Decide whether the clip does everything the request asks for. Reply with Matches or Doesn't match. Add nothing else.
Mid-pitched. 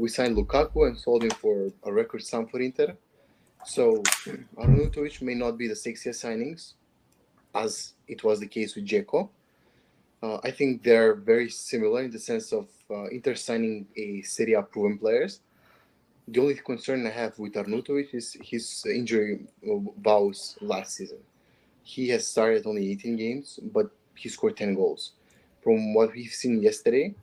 Doesn't match